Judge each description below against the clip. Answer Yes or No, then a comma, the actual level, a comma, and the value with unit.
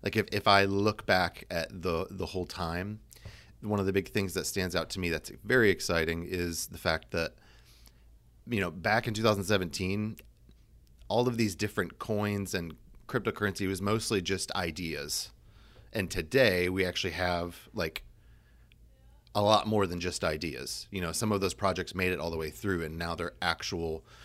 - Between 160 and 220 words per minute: Yes, average, 180 wpm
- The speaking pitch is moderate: No, very low, 95 Hz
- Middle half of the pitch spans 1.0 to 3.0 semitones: No, average, 3.4 semitones